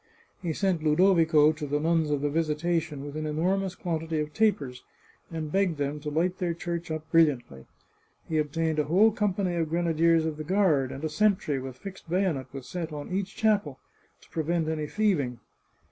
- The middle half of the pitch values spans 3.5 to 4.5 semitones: No, average, 3.1 semitones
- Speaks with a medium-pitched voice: Yes, medium, 160 Hz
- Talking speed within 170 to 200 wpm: Yes, average, 190 wpm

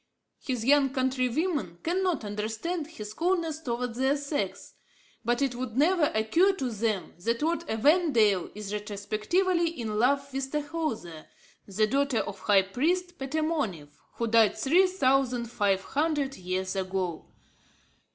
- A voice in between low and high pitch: No, very high, 255 Hz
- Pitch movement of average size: No, wide, 6.5 semitones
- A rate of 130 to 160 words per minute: Yes, slow, 135 wpm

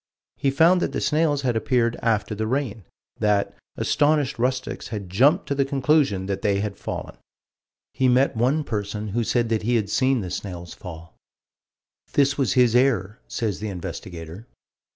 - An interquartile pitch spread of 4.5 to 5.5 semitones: Yes, average, 4.9 semitones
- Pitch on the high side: No, low, 115 Hz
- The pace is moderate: Yes, average, 170 wpm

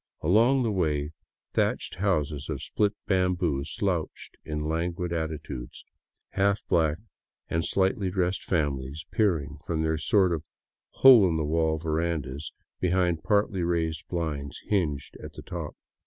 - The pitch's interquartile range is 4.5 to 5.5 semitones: No, average, 3.5 semitones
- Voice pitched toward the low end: Yes, very low, 85 Hz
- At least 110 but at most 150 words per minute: Yes, slow, 135 wpm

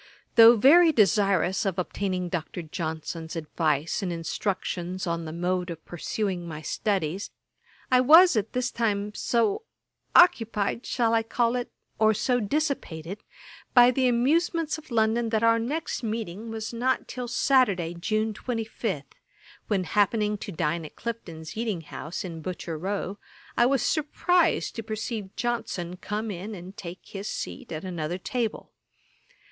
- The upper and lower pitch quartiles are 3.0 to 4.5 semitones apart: No, average, 5.1 semitones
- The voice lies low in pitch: No, high, 210 Hz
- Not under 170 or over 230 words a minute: No, average, 145 wpm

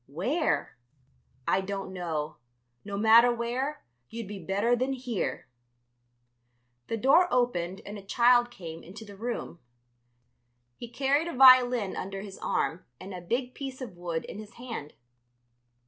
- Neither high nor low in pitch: No, high, 225 Hz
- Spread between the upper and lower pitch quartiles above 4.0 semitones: Yes, average, 4.6 semitones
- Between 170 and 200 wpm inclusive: No, average, 145 wpm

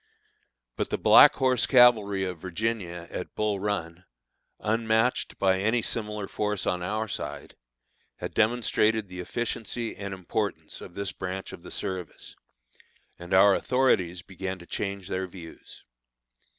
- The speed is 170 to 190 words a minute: No, slow, 135 wpm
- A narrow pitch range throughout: No, average, 3.2 semitones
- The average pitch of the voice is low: Yes, low, 100 Hz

